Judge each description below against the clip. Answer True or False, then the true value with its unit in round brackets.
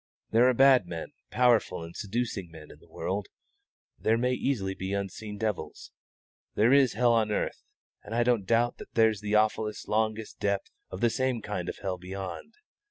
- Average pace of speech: True (185 wpm)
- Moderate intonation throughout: True (3.6 semitones)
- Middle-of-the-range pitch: False (110 Hz)